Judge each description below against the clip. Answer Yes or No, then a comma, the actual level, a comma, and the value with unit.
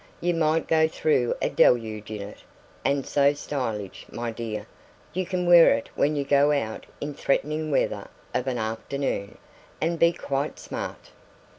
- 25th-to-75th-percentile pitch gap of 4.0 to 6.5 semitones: Yes, wide, 5.4 semitones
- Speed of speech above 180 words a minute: No, average, 160 wpm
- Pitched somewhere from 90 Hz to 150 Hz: Yes, medium, 140 Hz